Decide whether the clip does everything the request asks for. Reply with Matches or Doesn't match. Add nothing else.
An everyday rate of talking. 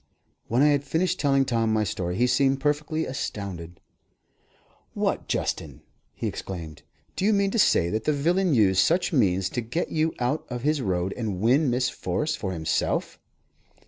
Matches